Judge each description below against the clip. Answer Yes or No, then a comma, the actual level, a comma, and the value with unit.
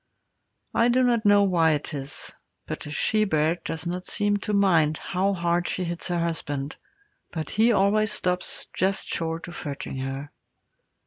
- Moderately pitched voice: Yes, medium, 175 Hz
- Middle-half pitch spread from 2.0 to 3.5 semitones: No, average, 4.2 semitones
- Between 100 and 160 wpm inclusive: No, average, 170 wpm